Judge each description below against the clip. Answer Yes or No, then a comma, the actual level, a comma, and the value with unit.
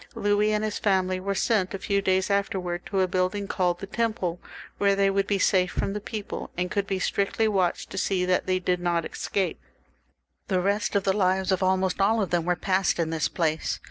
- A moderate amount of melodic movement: No, narrow, 1.7 semitones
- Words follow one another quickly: Yes, fast, 225 wpm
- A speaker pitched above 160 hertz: Yes, high, 190 Hz